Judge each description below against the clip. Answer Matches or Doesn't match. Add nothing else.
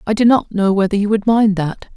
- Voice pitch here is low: Doesn't match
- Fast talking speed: Matches